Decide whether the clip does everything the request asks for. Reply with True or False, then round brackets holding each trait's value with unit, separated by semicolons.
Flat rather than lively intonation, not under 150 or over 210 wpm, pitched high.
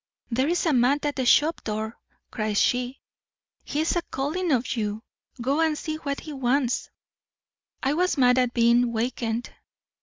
False (4.0 semitones; 155 wpm; 255 Hz)